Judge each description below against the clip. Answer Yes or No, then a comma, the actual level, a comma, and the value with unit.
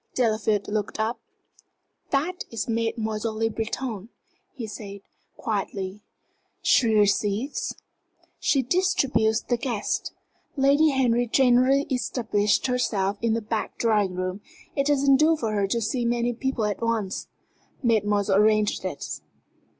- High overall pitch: Yes, high, 225 Hz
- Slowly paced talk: Yes, slow, 125 wpm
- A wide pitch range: No, average, 3.3 semitones